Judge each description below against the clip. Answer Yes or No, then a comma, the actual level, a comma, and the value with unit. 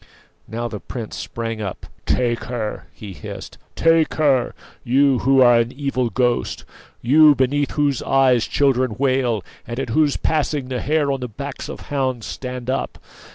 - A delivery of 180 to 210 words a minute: No, average, 160 wpm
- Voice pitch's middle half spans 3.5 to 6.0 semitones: No, average, 2.9 semitones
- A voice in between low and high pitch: No, low, 130 Hz